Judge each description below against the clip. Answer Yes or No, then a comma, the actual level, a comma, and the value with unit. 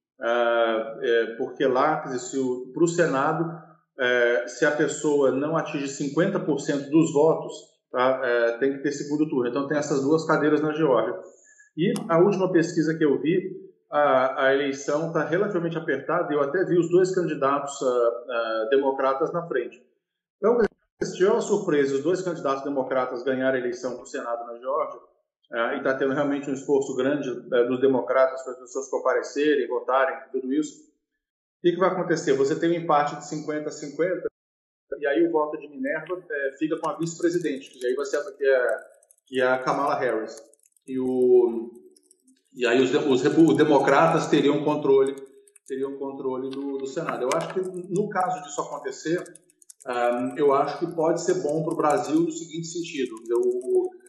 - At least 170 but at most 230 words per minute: Yes, average, 180 wpm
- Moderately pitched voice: Yes, medium, 150 Hz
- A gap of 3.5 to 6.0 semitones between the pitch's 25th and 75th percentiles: Yes, average, 5.2 semitones